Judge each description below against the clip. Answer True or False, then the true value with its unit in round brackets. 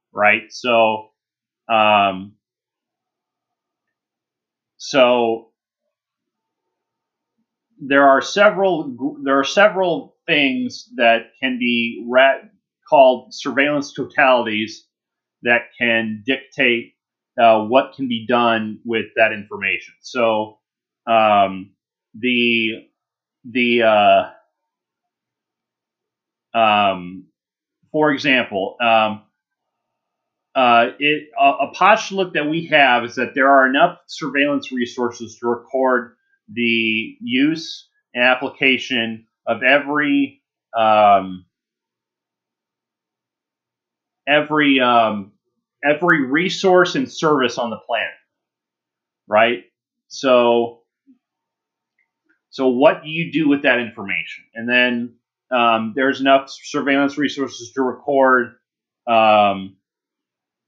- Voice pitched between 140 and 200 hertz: False (130 Hz)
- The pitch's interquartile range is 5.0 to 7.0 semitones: True (5.4 semitones)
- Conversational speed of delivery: False (90 wpm)